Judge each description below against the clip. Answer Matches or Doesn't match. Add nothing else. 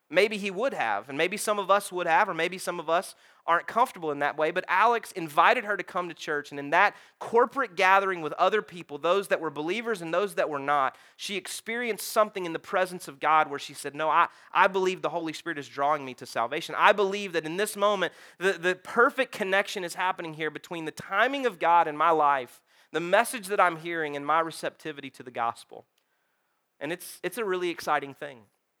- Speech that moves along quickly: Matches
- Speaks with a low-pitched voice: Doesn't match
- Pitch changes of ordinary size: Matches